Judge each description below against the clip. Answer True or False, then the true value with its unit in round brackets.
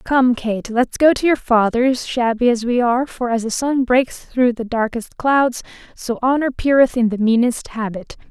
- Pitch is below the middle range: False (245 Hz)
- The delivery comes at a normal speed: True (195 wpm)